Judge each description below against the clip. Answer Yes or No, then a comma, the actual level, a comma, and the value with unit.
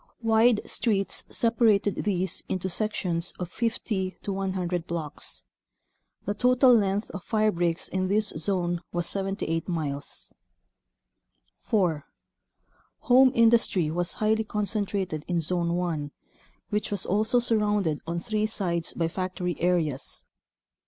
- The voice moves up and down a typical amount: Yes, average, 3.8 semitones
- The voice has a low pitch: No, high, 190 Hz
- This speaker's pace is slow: Yes, slow, 120 wpm